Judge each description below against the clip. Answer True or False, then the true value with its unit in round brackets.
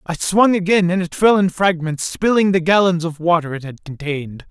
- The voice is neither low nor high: True (175 Hz)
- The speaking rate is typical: False (215 wpm)